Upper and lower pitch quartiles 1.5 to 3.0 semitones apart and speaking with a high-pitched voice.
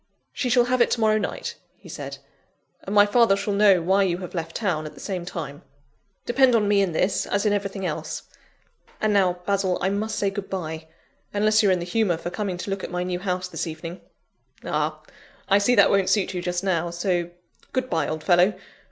Yes: average, 2.7 semitones; high, 195 Hz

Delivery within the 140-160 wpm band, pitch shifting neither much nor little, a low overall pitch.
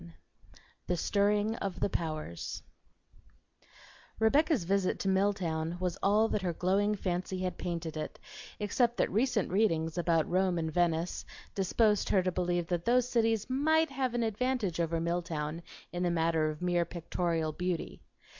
No: average, 155 wpm; average, 3.8 semitones; medium, 180 Hz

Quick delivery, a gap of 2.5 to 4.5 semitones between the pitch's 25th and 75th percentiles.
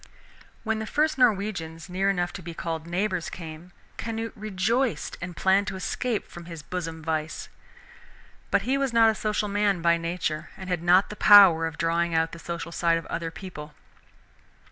No: average, 180 wpm; average, 4.0 semitones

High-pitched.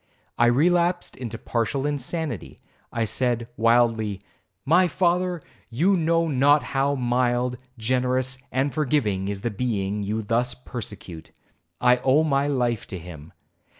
No: low, 125 Hz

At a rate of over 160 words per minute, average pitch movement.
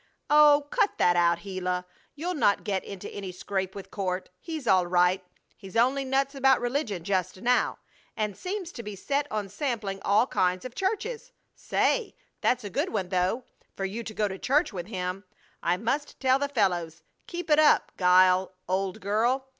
No: average, 180 wpm; wide, 6.7 semitones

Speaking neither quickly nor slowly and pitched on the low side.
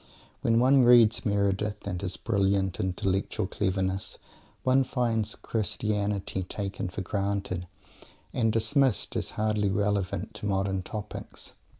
No: slow, 115 wpm; low, 100 Hz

